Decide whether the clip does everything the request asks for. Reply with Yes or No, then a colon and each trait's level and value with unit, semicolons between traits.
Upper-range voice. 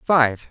No: low, 130 Hz